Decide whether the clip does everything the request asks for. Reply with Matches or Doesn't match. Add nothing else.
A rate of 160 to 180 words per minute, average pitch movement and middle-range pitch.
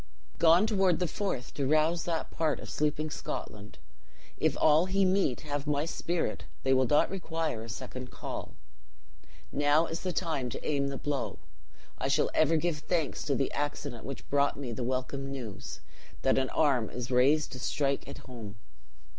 Matches